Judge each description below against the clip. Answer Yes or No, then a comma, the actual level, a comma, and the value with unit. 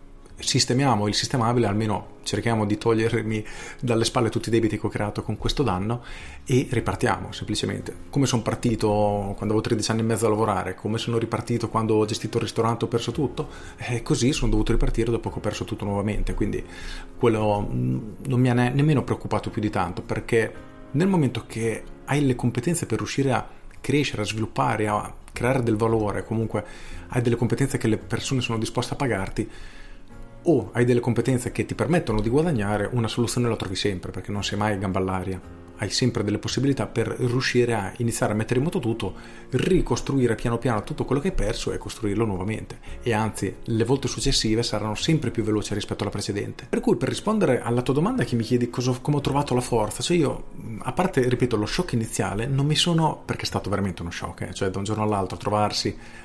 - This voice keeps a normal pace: No, fast, 200 wpm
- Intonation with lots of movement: No, average, 2.9 semitones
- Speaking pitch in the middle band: No, low, 115 Hz